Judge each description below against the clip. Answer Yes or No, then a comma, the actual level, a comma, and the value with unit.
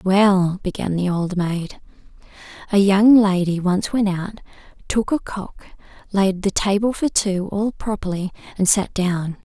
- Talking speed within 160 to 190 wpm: No, average, 150 wpm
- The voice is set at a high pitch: Yes, high, 195 Hz